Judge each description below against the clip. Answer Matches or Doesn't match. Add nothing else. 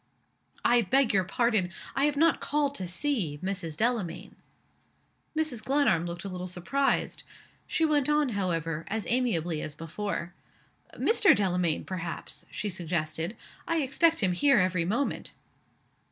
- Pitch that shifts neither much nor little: Doesn't match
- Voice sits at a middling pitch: Doesn't match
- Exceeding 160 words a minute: Doesn't match